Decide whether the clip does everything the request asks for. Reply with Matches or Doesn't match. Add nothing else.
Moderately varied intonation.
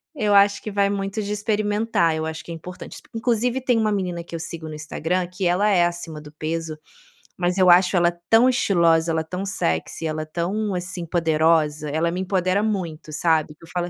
Matches